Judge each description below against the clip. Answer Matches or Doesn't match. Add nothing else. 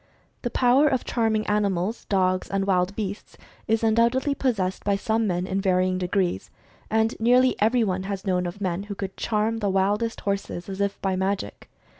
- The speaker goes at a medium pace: Matches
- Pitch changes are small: Doesn't match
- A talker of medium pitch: Doesn't match